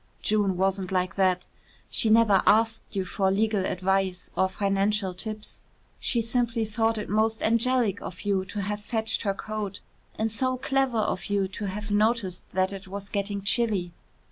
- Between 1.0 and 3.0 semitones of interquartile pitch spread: Yes, narrow, 2.5 semitones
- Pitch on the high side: Yes, high, 205 Hz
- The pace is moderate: Yes, average, 170 wpm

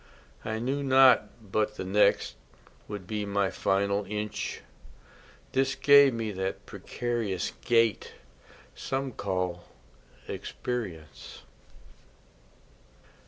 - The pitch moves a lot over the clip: No, average, 4.1 semitones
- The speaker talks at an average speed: No, slow, 90 wpm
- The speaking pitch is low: Yes, low, 105 Hz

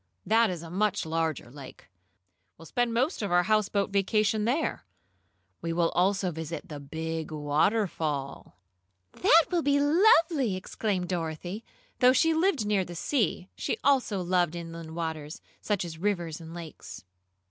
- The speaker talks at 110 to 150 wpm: Yes, average, 145 wpm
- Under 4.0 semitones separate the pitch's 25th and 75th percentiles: No, wide, 5.4 semitones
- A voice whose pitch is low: No, medium, 180 Hz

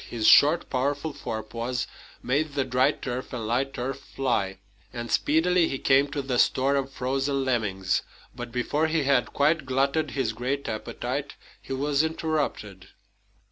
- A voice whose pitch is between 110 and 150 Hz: Yes, low, 135 Hz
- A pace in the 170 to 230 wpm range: No, average, 150 wpm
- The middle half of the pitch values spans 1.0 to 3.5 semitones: Yes, average, 2.8 semitones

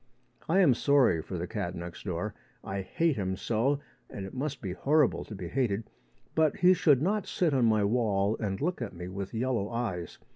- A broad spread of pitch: Yes, wide, 6.6 semitones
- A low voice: Yes, low, 110 Hz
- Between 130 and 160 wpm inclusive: No, fast, 205 wpm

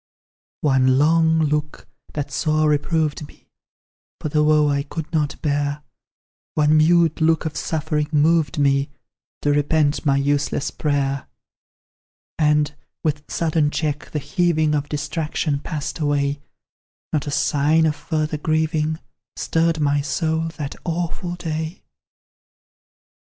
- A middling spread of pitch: No, narrow, 1.6 semitones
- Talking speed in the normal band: No, slow, 125 wpm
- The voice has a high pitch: No, medium, 150 Hz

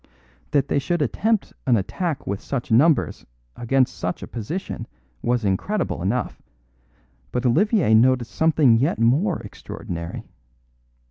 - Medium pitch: No, low, 125 Hz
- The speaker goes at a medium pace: No, slow, 125 wpm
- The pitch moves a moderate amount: No, wide, 6.1 semitones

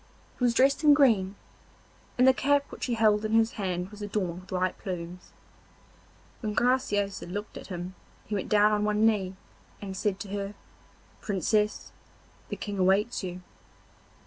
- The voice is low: No, high, 205 Hz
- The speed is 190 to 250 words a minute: No, average, 165 wpm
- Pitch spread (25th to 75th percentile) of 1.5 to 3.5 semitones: Yes, average, 2.9 semitones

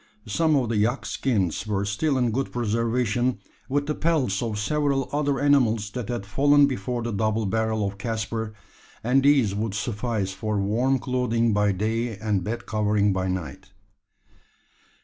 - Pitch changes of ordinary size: Yes, average, 3.7 semitones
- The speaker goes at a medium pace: Yes, average, 160 wpm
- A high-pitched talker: No, low, 115 Hz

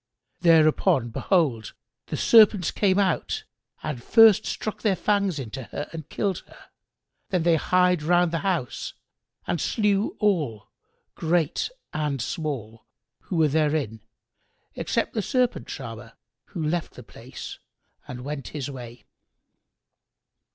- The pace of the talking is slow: Yes, slow, 130 wpm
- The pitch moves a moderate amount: No, wide, 5.7 semitones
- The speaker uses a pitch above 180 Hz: No, medium, 160 Hz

